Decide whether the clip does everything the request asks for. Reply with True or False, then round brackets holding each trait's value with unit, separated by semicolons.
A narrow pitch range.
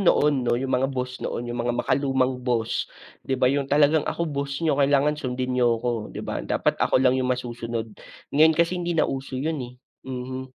True (2.2 semitones)